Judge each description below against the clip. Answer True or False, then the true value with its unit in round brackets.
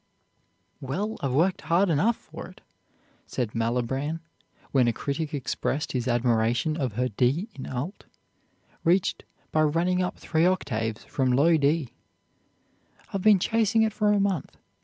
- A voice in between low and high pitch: True (150 Hz)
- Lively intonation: True (6.4 semitones)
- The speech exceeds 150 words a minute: False (145 wpm)